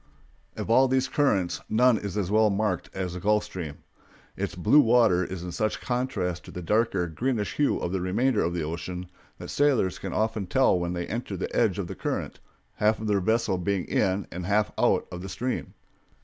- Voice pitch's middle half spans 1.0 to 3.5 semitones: No, average, 4.1 semitones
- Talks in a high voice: No, low, 100 Hz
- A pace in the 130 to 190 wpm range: No, fast, 205 wpm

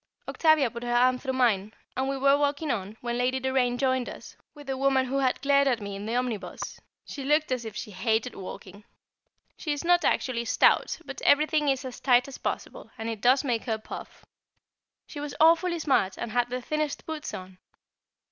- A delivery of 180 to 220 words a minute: Yes, fast, 205 wpm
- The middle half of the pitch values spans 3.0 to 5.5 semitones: Yes, average, 3.3 semitones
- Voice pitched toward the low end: No, very high, 255 Hz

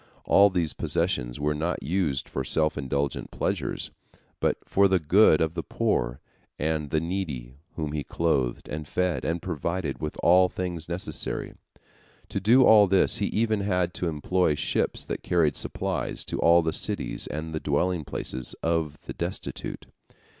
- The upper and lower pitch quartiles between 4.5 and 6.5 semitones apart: No, average, 3.7 semitones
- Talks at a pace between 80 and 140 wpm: No, average, 160 wpm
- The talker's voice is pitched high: No, very low, 80 Hz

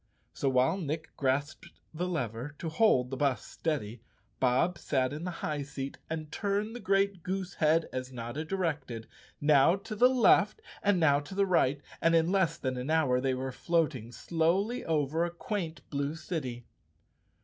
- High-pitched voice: No, medium, 155 Hz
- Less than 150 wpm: No, average, 170 wpm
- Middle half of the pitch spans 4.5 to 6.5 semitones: Yes, average, 5.2 semitones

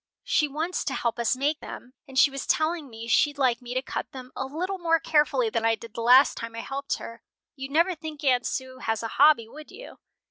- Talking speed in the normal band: No, fast, 240 wpm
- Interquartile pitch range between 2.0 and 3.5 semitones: No, average, 4.4 semitones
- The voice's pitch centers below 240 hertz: No, very high, 275 Hz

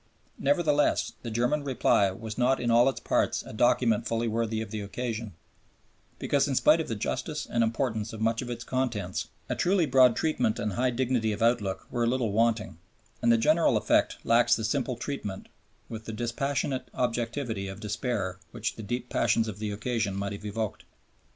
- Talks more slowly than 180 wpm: No, average, 190 wpm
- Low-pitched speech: Yes, low, 115 Hz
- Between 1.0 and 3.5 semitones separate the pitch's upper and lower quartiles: Yes, average, 2.8 semitones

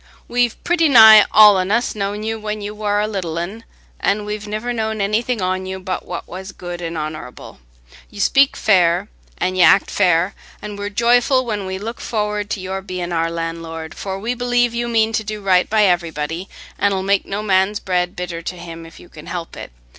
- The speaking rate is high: Yes, fast, 210 wpm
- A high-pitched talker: Yes, high, 200 Hz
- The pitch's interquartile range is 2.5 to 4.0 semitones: Yes, average, 3.3 semitones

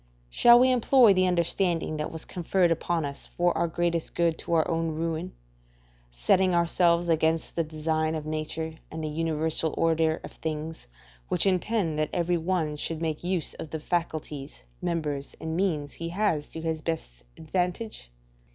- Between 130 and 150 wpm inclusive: No, average, 170 wpm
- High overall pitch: No, medium, 165 Hz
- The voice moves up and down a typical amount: No, narrow, 1.9 semitones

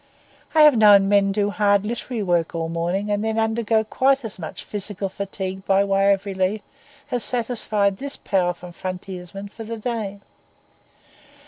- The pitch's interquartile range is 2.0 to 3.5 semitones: Yes, narrow, 2.6 semitones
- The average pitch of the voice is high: Yes, high, 200 Hz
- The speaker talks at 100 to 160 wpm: Yes, average, 155 wpm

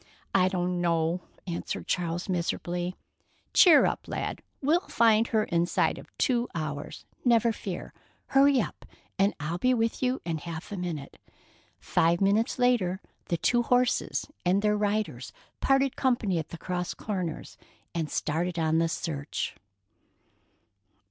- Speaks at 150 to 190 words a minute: No, average, 140 wpm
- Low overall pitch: No, medium, 180 Hz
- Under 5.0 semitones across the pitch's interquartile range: No, wide, 5.5 semitones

